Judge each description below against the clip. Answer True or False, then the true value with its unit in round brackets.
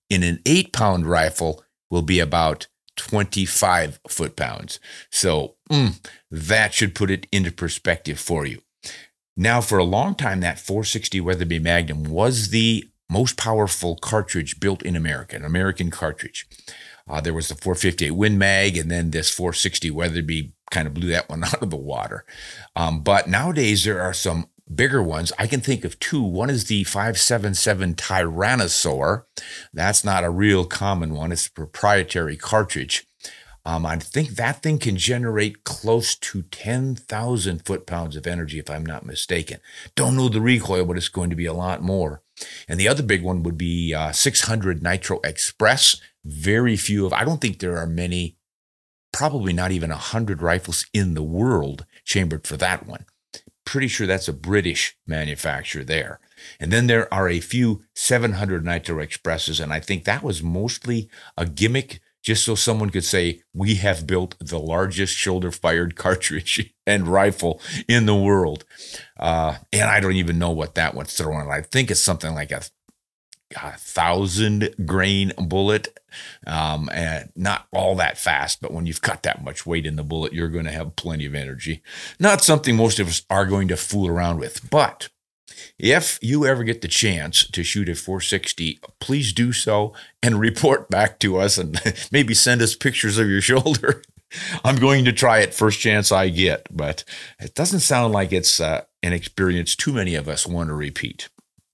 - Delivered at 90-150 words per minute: False (175 wpm)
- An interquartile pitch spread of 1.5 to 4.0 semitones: False (4.5 semitones)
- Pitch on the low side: True (95 Hz)